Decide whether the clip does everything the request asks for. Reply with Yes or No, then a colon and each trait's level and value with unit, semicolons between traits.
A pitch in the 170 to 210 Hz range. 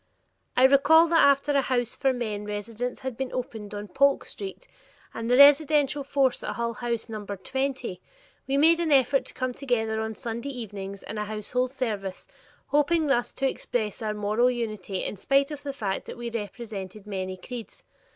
No: high, 245 Hz